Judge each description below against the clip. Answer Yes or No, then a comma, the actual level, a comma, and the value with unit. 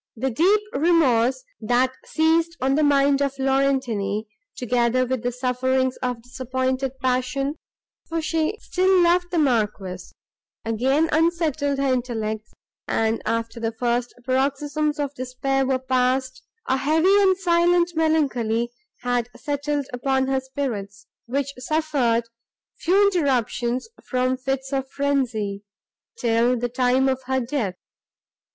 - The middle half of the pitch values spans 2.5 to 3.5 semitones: Yes, average, 3.1 semitones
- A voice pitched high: Yes, very high, 260 Hz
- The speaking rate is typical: No, slow, 125 wpm